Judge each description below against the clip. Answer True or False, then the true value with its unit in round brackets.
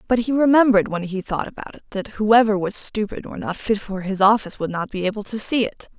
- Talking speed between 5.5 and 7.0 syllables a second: True (6.0 syllables/s)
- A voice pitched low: False (210 Hz)